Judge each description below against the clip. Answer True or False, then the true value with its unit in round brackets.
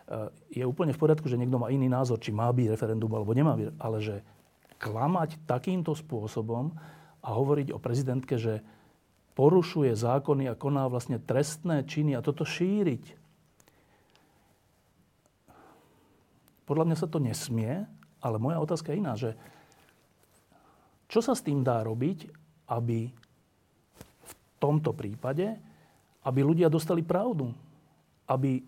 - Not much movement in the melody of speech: False (5.0 semitones)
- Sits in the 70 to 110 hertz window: False (135 Hz)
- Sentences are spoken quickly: False (130 wpm)